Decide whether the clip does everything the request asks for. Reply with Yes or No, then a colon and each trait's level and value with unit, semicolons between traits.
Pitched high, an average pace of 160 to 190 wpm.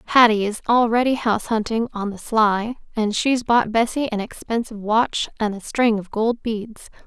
Yes: high, 225 Hz; average, 180 wpm